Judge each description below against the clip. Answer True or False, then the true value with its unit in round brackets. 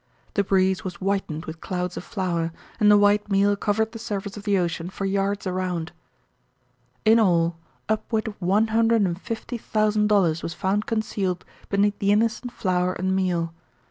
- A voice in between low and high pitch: False (195 Hz)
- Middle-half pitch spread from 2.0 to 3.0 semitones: True (2.7 semitones)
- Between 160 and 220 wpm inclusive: True (175 wpm)